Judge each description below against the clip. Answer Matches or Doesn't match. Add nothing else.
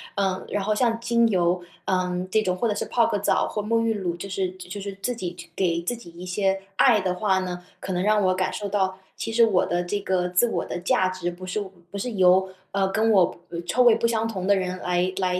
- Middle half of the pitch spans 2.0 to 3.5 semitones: Matches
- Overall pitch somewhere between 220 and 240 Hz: Doesn't match